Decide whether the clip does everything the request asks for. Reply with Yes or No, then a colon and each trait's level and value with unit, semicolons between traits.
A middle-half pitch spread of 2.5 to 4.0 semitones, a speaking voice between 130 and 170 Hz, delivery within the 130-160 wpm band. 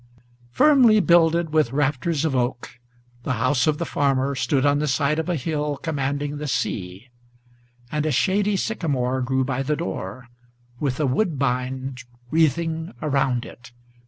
Yes: average, 3.7 semitones; medium, 140 Hz; average, 150 wpm